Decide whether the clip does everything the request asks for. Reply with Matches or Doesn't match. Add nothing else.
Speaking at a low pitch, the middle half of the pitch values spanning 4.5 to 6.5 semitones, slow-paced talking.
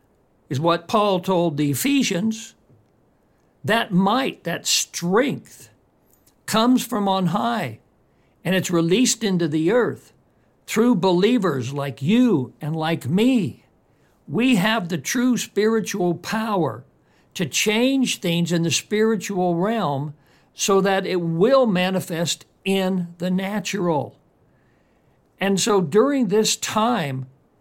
Doesn't match